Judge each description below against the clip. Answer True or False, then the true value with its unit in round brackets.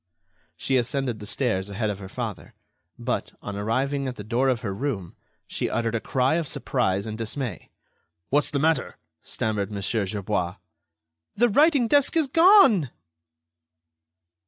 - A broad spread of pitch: True (5.7 semitones)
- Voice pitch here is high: False (120 Hz)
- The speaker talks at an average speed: True (150 wpm)